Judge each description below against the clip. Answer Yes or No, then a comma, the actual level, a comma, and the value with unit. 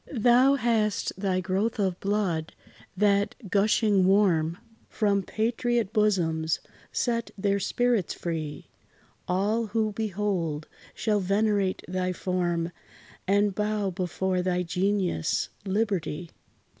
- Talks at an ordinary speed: No, slow, 105 wpm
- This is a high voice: Yes, high, 200 Hz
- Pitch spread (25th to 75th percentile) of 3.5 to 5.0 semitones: No, average, 2.9 semitones